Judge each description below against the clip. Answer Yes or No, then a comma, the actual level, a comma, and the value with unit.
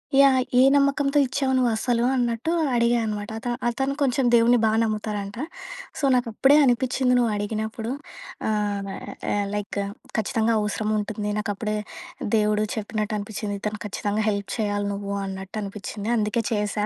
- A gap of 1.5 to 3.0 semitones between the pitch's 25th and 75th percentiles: Yes, average, 2.7 semitones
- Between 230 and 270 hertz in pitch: No, high, 215 Hz